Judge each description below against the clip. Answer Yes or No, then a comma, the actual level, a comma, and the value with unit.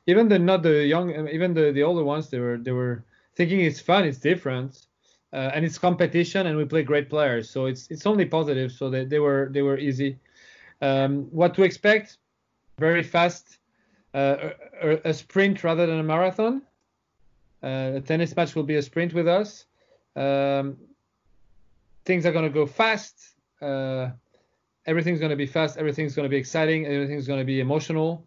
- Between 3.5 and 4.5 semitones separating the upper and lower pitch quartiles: Yes, average, 3.8 semitones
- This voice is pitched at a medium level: Yes, medium, 155 Hz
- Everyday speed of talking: Yes, average, 180 wpm